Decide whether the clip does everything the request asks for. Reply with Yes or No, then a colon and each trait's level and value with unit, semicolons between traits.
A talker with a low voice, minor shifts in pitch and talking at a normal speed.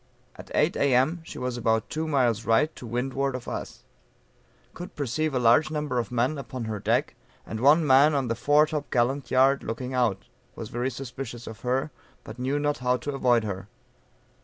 No: low, 130 Hz; average, 3.3 semitones; average, 190 wpm